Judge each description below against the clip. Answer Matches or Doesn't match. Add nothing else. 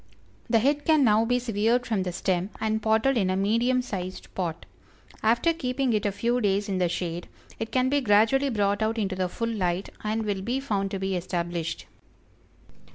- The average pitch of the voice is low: Doesn't match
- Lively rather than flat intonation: Doesn't match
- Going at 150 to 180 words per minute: Doesn't match